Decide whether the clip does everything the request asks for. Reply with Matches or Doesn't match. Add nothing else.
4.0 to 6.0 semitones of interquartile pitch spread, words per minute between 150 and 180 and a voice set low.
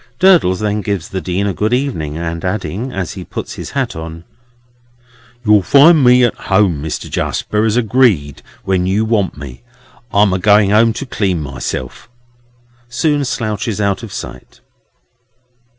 Matches